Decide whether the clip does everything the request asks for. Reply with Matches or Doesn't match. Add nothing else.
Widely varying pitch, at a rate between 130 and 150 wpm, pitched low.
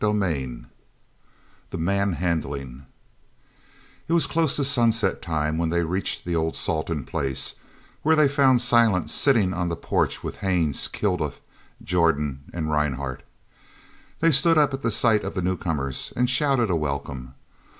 Matches